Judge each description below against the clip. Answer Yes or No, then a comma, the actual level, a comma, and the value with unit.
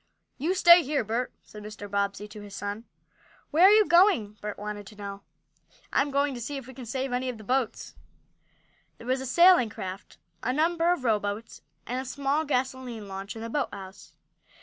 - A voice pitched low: No, high, 245 Hz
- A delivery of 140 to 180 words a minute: No, average, 195 wpm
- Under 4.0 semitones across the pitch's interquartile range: No, average, 5.3 semitones